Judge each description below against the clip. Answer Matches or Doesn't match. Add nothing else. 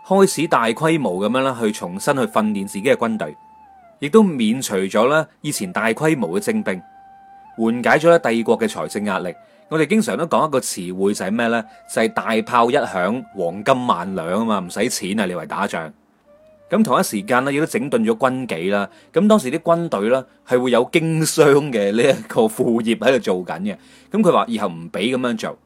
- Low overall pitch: Doesn't match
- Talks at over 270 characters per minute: Matches